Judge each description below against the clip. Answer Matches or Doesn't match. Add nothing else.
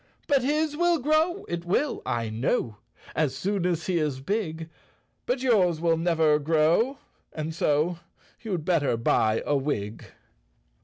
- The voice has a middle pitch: Matches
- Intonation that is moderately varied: Doesn't match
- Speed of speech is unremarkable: Matches